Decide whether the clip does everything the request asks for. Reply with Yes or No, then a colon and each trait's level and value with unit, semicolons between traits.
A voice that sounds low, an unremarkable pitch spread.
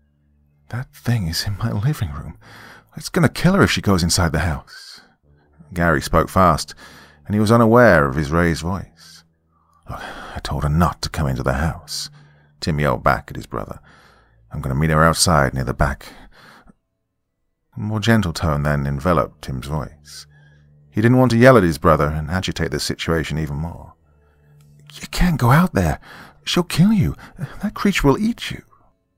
No: very low, 80 Hz; wide, 6.5 semitones